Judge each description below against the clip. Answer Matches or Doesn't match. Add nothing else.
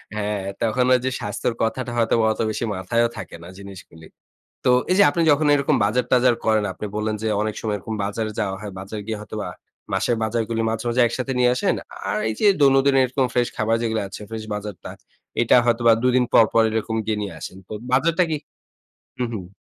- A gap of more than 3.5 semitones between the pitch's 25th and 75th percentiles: Doesn't match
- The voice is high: Doesn't match